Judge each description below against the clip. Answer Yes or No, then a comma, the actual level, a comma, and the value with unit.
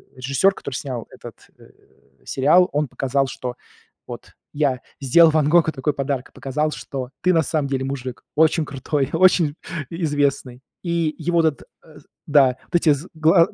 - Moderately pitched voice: Yes, medium, 145 Hz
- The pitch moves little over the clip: No, average, 3.2 semitones